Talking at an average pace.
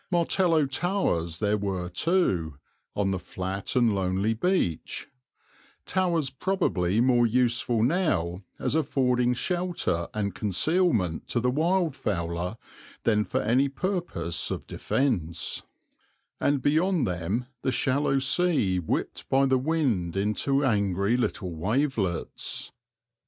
No: slow, 115 wpm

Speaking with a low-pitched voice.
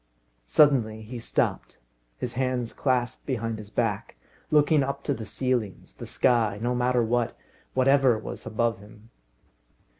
Yes: low, 120 Hz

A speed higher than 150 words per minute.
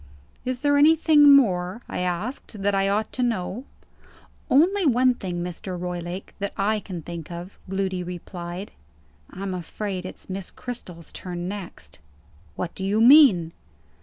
No: average, 145 wpm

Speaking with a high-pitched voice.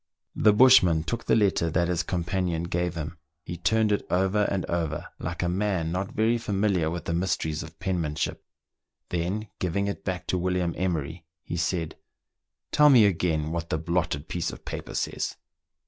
No: very low, 90 Hz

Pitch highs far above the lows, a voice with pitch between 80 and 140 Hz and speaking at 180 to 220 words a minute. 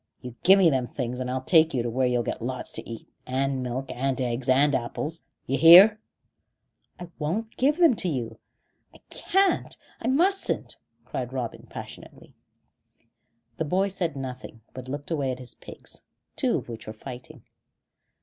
No: wide, 5.8 semitones; low, 135 Hz; average, 170 wpm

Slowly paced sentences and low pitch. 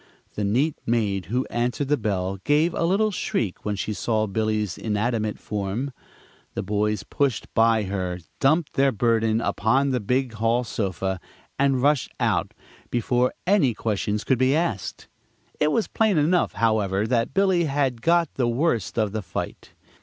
No: average, 160 wpm; low, 115 Hz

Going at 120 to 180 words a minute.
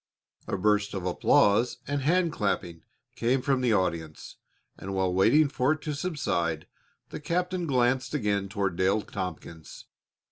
Yes: average, 145 wpm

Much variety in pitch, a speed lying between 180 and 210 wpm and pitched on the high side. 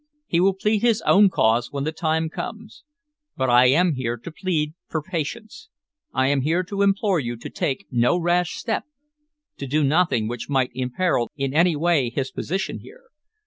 No: wide, 6.1 semitones; average, 185 wpm; medium, 160 Hz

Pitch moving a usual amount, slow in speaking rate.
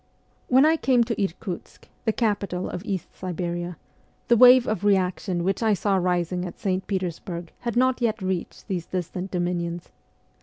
No: average, 3.7 semitones; average, 165 wpm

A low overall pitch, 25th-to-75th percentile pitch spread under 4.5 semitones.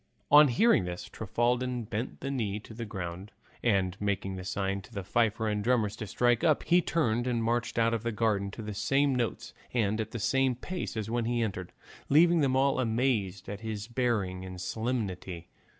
Yes: low, 115 Hz; average, 3.8 semitones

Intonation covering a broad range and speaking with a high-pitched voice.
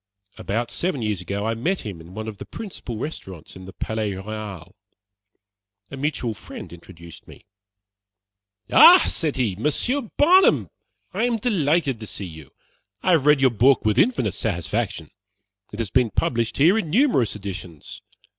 No: wide, 7.3 semitones; low, 115 Hz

